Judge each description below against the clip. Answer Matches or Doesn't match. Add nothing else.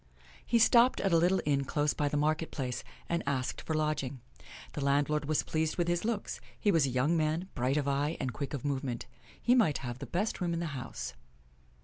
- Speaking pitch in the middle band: Matches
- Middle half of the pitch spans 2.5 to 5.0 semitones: Matches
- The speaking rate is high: Matches